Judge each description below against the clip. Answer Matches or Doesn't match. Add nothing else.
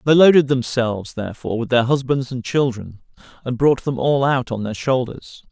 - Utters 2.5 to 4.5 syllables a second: Doesn't match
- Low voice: Matches